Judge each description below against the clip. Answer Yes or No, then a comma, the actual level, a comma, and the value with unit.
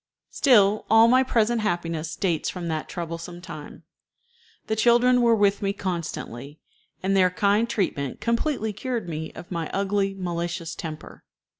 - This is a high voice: Yes, high, 195 Hz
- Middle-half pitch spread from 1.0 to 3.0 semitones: No, average, 4.7 semitones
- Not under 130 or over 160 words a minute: Yes, average, 145 wpm